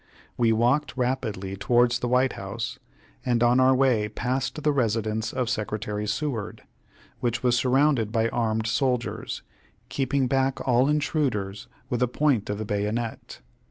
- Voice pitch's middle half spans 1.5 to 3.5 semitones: Yes, average, 3.1 semitones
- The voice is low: Yes, low, 120 Hz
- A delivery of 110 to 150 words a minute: Yes, average, 145 wpm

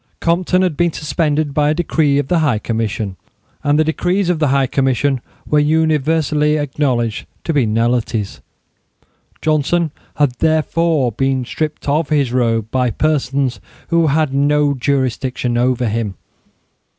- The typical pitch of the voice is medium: Yes, medium, 145 Hz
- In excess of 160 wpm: No, average, 140 wpm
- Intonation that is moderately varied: Yes, average, 3.8 semitones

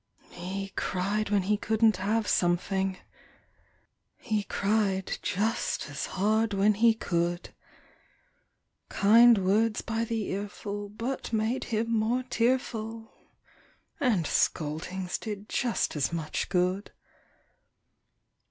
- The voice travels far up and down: No, average, 3.0 semitones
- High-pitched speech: Yes, high, 205 Hz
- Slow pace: Yes, slow, 105 wpm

